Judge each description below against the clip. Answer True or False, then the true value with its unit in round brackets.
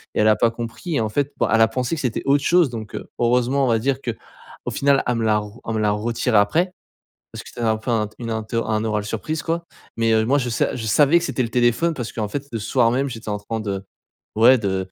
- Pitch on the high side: False (115 Hz)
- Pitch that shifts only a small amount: False (3.6 semitones)